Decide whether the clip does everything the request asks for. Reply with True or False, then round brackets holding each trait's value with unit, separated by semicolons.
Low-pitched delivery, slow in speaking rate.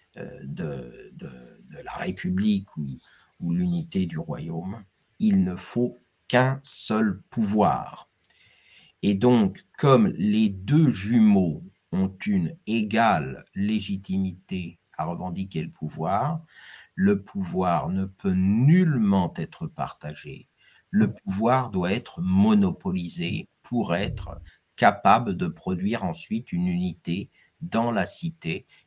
True (115 Hz; 110 wpm)